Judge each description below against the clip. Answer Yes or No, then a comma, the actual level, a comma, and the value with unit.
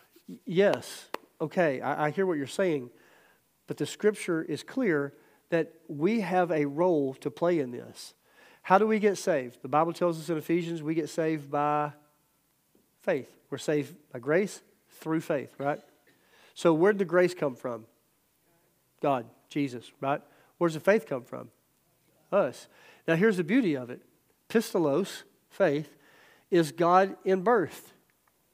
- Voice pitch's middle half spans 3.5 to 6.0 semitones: Yes, average, 3.9 semitones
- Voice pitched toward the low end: No, medium, 165 Hz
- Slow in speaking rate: No, average, 150 wpm